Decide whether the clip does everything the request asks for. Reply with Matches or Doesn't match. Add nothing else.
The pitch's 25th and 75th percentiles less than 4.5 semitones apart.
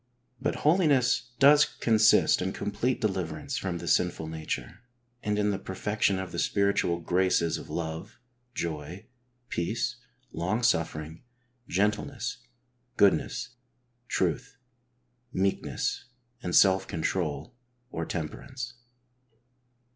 Doesn't match